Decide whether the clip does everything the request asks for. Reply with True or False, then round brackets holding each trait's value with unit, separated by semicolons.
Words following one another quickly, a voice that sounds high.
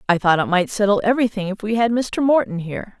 True (240 wpm; 210 Hz)